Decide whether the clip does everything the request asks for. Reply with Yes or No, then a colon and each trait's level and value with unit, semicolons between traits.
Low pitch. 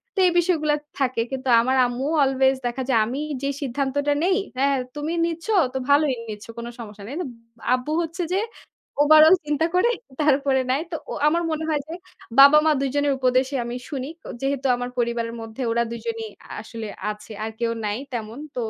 No: very high, 270 Hz